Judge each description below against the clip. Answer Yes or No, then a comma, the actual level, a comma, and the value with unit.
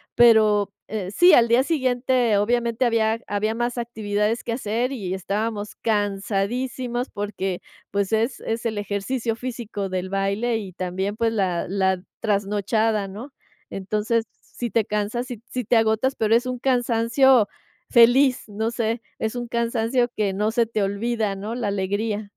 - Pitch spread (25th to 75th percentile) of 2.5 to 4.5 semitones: Yes, average, 2.8 semitones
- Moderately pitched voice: No, high, 220 Hz